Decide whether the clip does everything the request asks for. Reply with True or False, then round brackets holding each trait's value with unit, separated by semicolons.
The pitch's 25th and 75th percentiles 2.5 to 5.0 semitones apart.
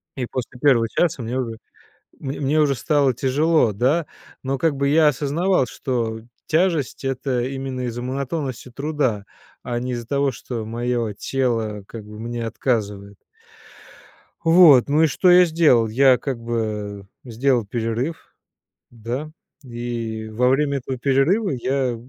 True (3.5 semitones)